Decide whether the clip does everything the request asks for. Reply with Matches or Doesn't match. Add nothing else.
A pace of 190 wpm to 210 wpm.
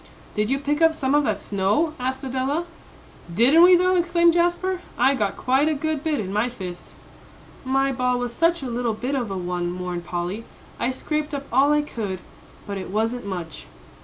Matches